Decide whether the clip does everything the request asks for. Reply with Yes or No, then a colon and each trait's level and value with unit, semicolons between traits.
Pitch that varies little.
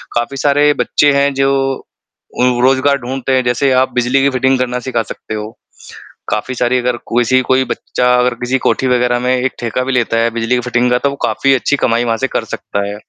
Yes: narrow, 1.6 semitones